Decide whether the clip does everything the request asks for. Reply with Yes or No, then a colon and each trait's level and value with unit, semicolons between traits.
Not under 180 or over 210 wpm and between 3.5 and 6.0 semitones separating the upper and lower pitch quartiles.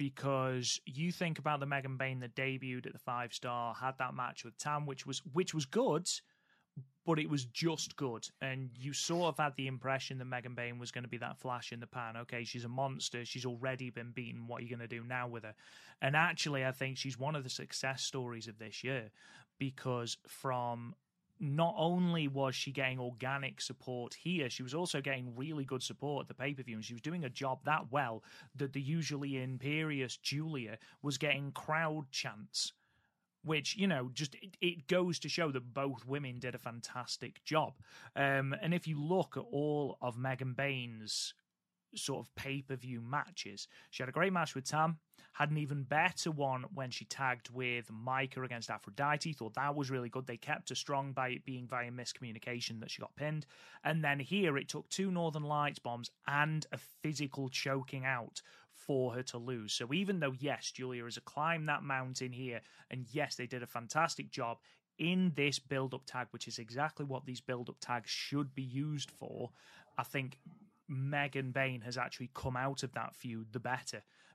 No: average, 200 wpm; average, 3.0 semitones